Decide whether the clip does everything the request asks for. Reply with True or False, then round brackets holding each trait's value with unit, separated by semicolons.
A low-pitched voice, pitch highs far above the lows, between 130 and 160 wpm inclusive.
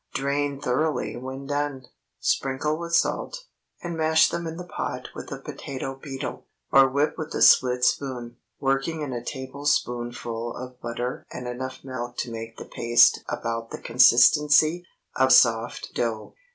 False (130 Hz; 3.1 semitones; 150 wpm)